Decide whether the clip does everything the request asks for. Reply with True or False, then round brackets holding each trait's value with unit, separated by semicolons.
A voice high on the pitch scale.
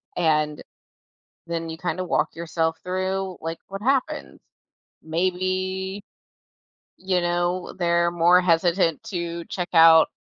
False (175 Hz)